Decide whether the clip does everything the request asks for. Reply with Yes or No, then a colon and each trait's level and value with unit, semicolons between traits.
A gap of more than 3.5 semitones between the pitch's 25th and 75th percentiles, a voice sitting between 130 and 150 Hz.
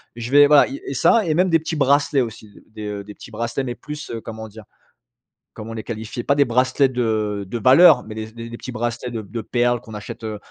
No: average, 4.1 semitones; low, 120 Hz